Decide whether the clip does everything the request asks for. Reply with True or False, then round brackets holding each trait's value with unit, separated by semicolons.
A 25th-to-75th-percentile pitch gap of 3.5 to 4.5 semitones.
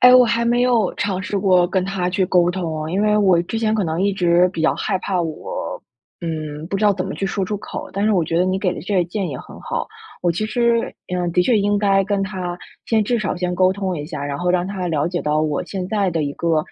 False (3.0 semitones)